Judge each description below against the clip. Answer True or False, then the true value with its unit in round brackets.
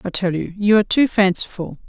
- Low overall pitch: False (195 Hz)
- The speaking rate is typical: False (225 wpm)